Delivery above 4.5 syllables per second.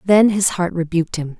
Yes: 5.4 syllables/s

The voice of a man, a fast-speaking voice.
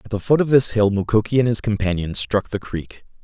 Yes: male; fast, 240 wpm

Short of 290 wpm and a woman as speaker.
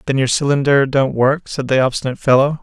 No: fast, 205 wpm; male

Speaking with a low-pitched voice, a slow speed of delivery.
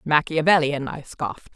No: medium, 145 Hz; slow, 115 wpm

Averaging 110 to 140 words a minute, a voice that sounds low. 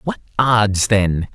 Yes: slow, 135 wpm; low, 110 Hz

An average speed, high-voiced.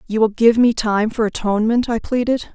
No: fast, 210 wpm; high, 225 Hz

